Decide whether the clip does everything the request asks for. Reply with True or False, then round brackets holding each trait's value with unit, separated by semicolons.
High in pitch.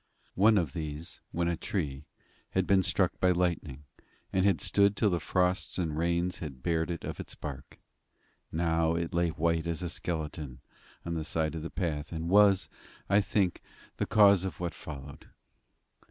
False (85 Hz)